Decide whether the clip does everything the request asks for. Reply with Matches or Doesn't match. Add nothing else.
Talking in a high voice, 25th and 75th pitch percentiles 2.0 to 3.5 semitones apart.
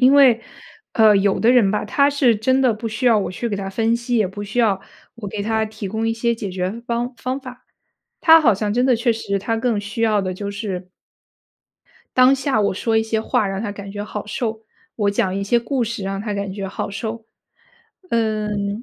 Matches